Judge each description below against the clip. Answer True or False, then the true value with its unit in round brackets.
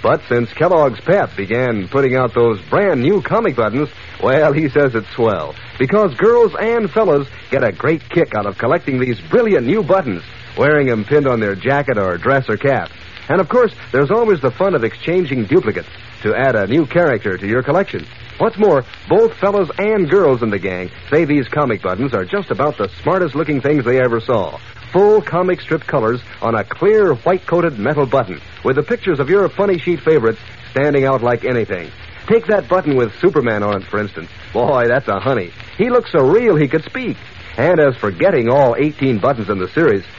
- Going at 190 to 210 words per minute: True (205 wpm)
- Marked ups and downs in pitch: True (7.8 semitones)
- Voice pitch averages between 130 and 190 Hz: True (140 Hz)